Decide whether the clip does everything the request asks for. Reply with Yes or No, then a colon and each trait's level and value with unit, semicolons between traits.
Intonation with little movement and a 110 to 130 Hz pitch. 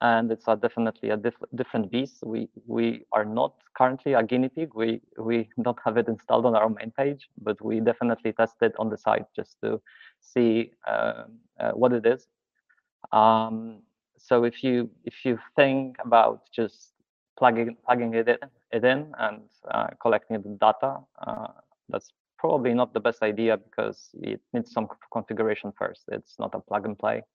Yes: narrow, 1.9 semitones; low, 115 Hz